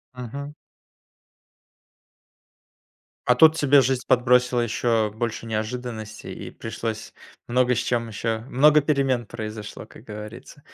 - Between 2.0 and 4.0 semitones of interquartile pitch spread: Yes, average, 2.9 semitones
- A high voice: No, low, 120 Hz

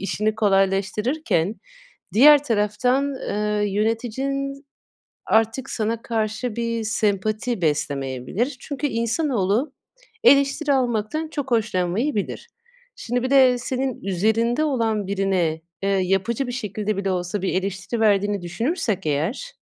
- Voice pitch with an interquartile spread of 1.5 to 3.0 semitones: No, average, 4.7 semitones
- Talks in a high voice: Yes, high, 220 Hz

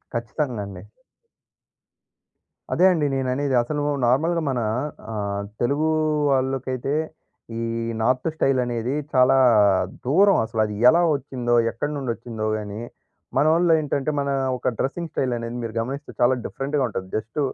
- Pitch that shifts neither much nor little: Yes, average, 3.6 semitones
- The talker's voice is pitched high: No, low, 130 Hz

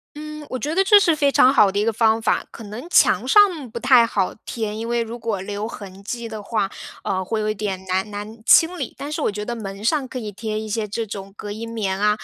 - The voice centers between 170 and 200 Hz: No, high, 220 Hz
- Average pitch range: Yes, average, 3.6 semitones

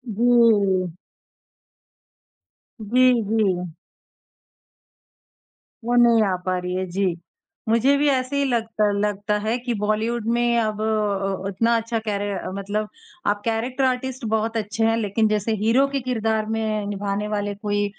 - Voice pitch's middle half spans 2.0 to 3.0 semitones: Yes, narrow, 2.5 semitones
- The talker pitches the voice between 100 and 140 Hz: No, high, 215 Hz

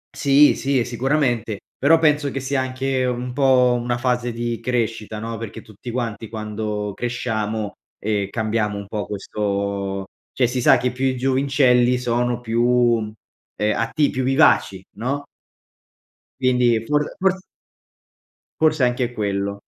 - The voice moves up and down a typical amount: Yes, average, 3.2 semitones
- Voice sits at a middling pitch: No, low, 120 Hz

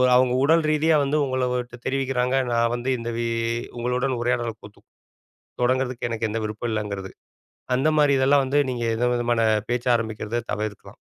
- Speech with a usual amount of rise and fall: No, narrow, 2.2 semitones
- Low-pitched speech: Yes, low, 120 Hz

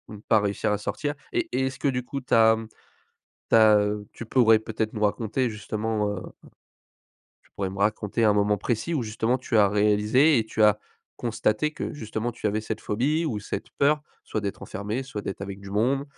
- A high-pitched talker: No, low, 110 Hz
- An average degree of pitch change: Yes, average, 3.2 semitones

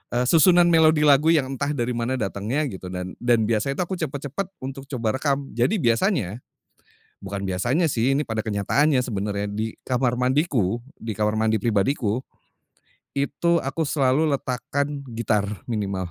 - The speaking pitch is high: No, low, 125 Hz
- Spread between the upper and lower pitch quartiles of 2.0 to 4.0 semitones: No, average, 4.9 semitones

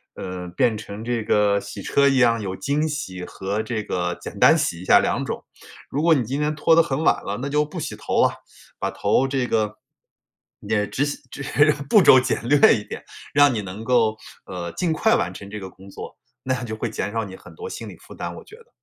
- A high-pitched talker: No, low, 115 Hz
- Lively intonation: Yes, wide, 5.9 semitones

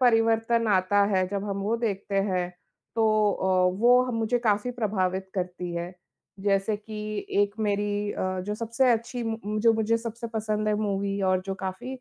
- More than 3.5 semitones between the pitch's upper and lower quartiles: No, narrow, 2.6 semitones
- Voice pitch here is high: Yes, high, 210 Hz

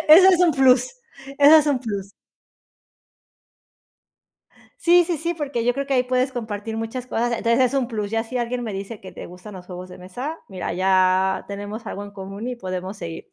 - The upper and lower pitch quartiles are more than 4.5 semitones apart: Yes, average, 5.0 semitones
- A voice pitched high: Yes, high, 225 Hz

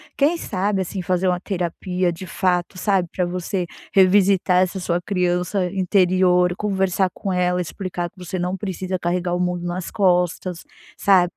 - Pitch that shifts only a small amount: Yes, narrow, 1.2 semitones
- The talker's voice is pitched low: No, medium, 180 Hz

